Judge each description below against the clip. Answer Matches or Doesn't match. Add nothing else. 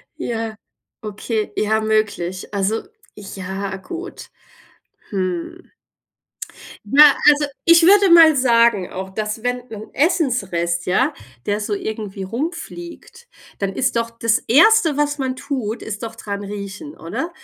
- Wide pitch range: Matches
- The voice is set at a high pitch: Matches